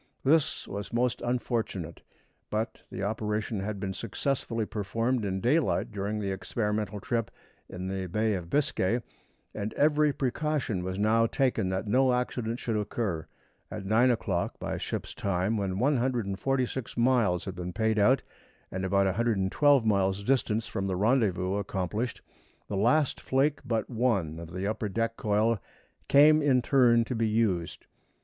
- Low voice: Yes, low, 110 Hz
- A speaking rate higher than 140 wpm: Yes, average, 150 wpm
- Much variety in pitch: No, average, 4.3 semitones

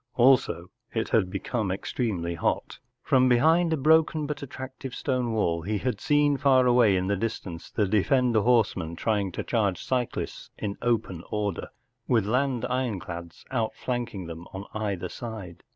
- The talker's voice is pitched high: No, low, 115 Hz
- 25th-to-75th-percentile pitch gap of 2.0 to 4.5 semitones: No, average, 5.1 semitones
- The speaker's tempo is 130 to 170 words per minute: Yes, average, 150 wpm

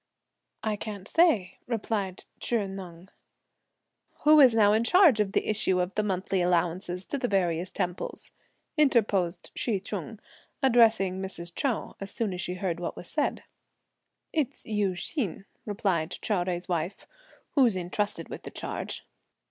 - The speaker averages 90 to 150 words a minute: Yes, average, 145 wpm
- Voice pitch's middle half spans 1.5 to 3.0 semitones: No, average, 3.8 semitones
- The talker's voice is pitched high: Yes, high, 195 Hz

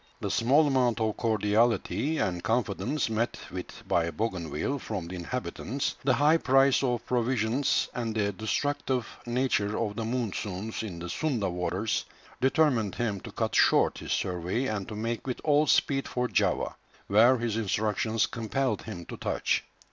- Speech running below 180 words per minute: Yes, average, 155 wpm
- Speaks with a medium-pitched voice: No, low, 115 Hz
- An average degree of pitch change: Yes, average, 4.0 semitones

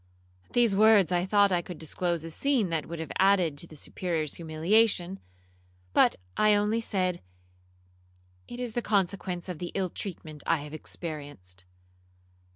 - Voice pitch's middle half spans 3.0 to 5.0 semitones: Yes, average, 4.2 semitones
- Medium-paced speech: Yes, average, 160 wpm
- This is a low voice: No, medium, 180 Hz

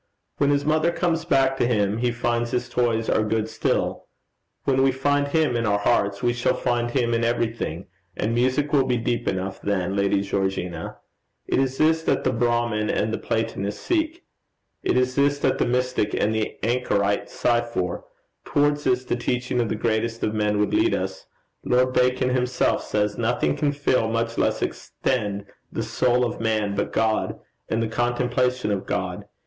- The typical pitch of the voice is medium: No, low, 120 Hz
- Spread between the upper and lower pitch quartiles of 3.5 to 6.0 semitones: No, average, 3.1 semitones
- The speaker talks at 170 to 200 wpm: Yes, average, 185 wpm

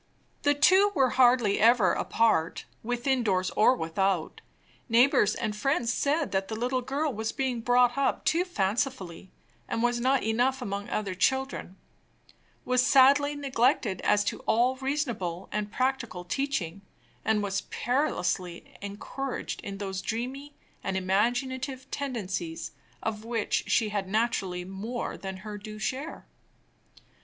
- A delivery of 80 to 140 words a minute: Yes, slow, 135 wpm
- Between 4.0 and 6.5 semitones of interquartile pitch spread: Yes, average, 4.9 semitones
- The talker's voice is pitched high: Yes, high, 230 Hz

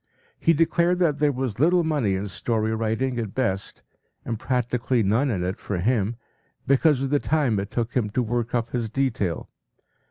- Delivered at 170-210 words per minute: Yes, average, 185 wpm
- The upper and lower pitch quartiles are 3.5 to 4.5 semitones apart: Yes, average, 4.1 semitones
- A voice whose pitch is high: No, low, 120 Hz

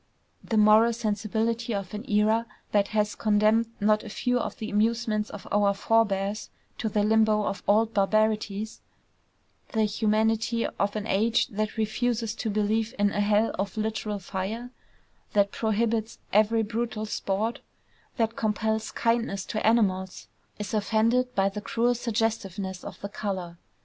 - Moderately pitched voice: No, high, 215 Hz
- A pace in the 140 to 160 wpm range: Yes, average, 145 wpm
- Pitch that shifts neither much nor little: No, narrow, 1.6 semitones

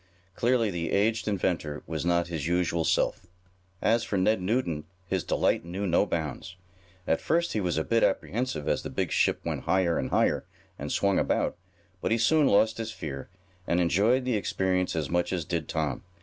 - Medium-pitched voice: No, very low, 90 Hz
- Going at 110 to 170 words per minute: No, average, 190 wpm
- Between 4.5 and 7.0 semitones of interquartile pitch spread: Yes, average, 4.8 semitones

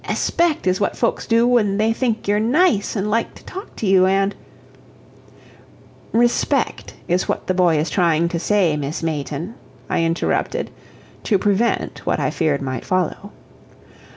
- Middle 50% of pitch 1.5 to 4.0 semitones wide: No, average, 5.1 semitones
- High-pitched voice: Yes, high, 195 Hz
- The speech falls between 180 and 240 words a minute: No, average, 160 wpm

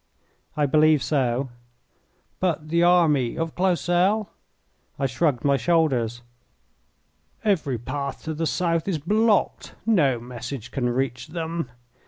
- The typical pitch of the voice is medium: Yes, medium, 155 Hz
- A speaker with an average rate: No, slow, 120 wpm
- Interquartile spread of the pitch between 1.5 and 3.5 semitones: No, average, 4.8 semitones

